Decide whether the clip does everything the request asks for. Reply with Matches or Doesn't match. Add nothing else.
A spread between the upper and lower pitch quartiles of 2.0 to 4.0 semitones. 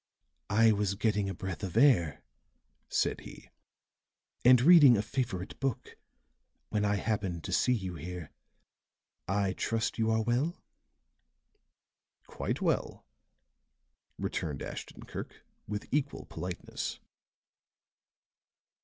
Doesn't match